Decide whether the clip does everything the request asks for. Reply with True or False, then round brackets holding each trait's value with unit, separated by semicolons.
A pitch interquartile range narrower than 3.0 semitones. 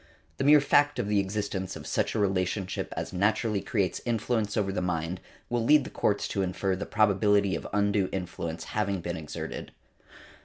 True (2.5 semitones)